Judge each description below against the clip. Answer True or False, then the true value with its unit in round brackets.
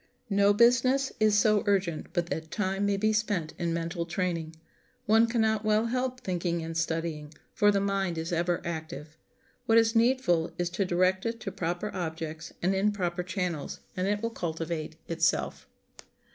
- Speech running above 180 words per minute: False (170 wpm)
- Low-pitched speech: False (185 Hz)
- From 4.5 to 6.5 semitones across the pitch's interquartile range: False (4.1 semitones)